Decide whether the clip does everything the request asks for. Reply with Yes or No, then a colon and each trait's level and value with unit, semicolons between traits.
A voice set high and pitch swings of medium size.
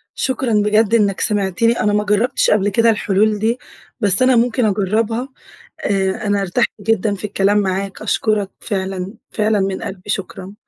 No: high, 205 Hz; narrow, 2.3 semitones